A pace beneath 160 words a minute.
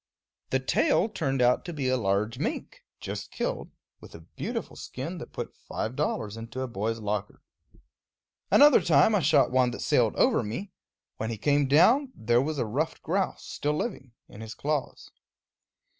No: average, 175 wpm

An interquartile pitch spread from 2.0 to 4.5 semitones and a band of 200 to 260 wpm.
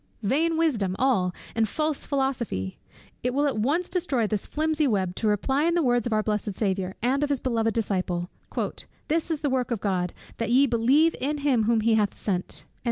No: wide, 5.5 semitones; fast, 205 wpm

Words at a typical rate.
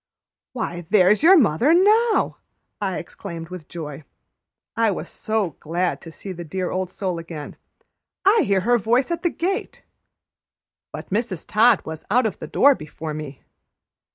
Yes: average, 155 wpm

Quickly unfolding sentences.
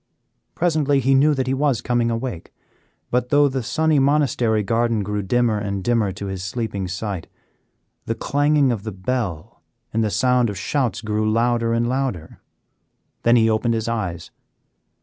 No: average, 165 wpm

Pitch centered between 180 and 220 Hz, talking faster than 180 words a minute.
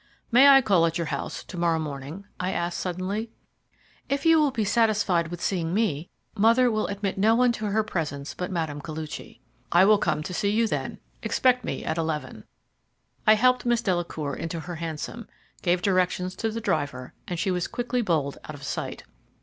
Yes: medium, 185 Hz; average, 190 wpm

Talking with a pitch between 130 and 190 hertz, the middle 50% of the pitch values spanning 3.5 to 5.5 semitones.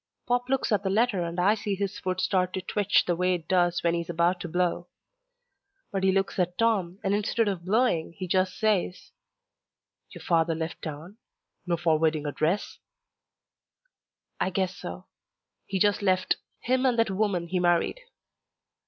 No: medium, 185 Hz; average, 2.9 semitones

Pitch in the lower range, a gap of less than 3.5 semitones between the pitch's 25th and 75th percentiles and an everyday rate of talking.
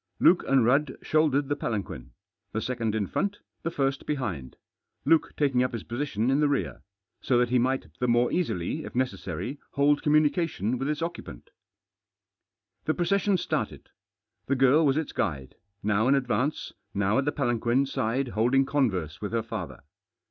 No: low, 130 Hz; average, 4.7 semitones; average, 165 wpm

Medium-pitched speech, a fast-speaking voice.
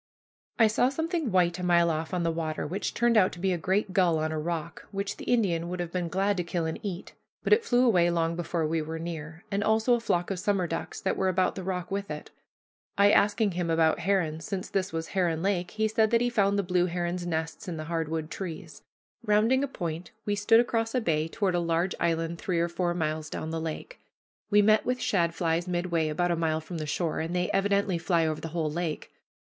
Yes: medium, 175 Hz; fast, 240 wpm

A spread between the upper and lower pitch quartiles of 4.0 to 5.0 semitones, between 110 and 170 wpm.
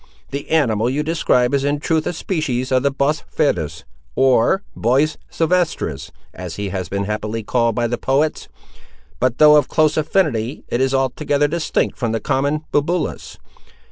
Yes: average, 4.6 semitones; average, 165 wpm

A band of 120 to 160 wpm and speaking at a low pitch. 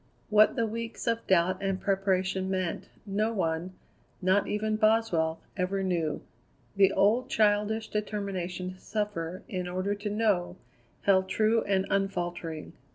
No: slow, 135 wpm; high, 195 Hz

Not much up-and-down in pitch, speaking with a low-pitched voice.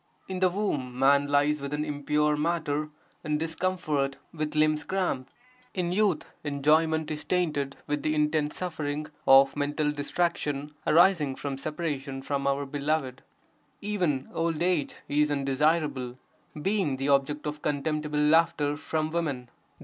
No: narrow, 2.2 semitones; medium, 150 Hz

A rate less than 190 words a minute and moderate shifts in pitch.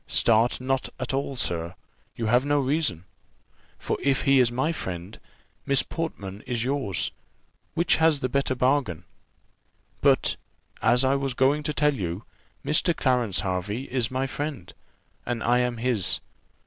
Yes: average, 150 wpm; average, 4.2 semitones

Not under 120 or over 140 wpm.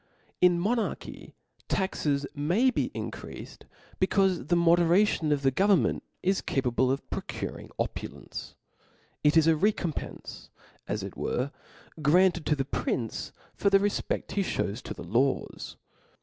Yes: slow, 135 wpm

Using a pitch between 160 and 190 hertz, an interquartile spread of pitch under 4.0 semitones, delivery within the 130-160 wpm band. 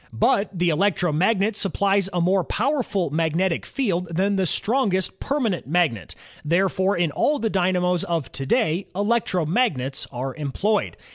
Yes: medium, 185 Hz; average, 3.5 semitones; slow, 135 wpm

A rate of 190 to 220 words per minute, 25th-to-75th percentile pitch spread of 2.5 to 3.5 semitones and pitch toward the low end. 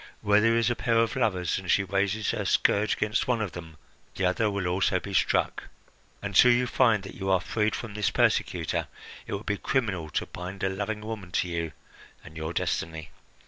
Yes: fast, 205 wpm; average, 3.2 semitones; low, 100 Hz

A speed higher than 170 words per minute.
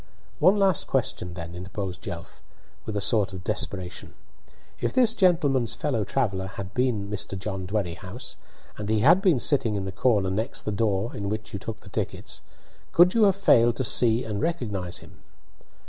Yes: average, 180 wpm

